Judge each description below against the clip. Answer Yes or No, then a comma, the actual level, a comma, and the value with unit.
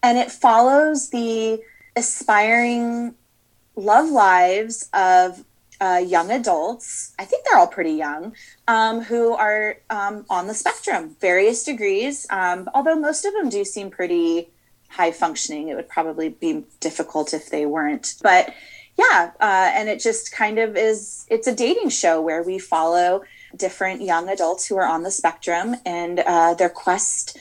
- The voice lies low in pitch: No, high, 210 Hz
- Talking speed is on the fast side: No, average, 160 wpm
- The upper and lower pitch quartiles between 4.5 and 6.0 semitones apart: Yes, average, 5.1 semitones